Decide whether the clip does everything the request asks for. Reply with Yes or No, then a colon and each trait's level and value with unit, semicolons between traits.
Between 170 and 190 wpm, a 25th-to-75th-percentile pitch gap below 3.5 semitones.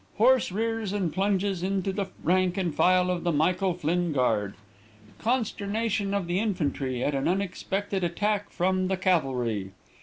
No: average, 150 wpm; average, 2.9 semitones